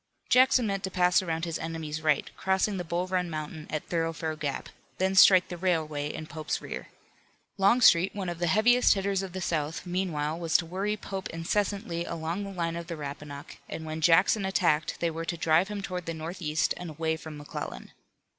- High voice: No, medium, 170 Hz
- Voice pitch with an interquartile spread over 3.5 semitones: No, average, 3.2 semitones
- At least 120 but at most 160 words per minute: No, average, 195 wpm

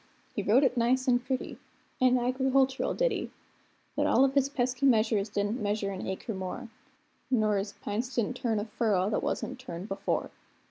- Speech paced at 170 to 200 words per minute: Yes, average, 175 wpm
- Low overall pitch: No, high, 240 Hz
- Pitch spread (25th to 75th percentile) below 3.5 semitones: No, average, 4.0 semitones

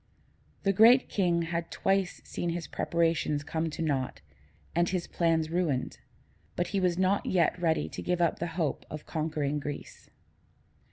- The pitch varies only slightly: Yes, narrow, 2.1 semitones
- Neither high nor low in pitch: Yes, medium, 170 Hz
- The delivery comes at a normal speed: Yes, average, 160 wpm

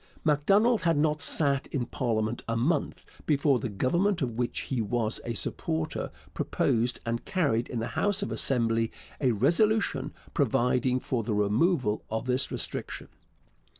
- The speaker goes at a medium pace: Yes, average, 150 wpm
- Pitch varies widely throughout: No, average, 4.6 semitones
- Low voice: Yes, low, 125 Hz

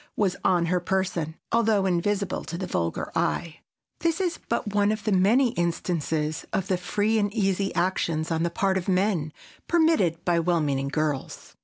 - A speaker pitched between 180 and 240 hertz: Yes, medium, 185 Hz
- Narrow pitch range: No, average, 3.7 semitones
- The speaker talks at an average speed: Yes, average, 175 wpm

